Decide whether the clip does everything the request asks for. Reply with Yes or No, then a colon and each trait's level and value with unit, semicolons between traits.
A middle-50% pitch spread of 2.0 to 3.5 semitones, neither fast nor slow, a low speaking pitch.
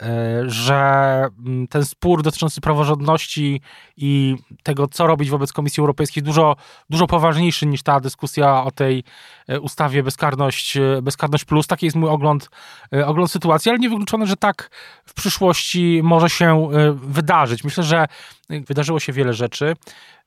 No: average, 2.8 semitones; average, 135 wpm; medium, 150 Hz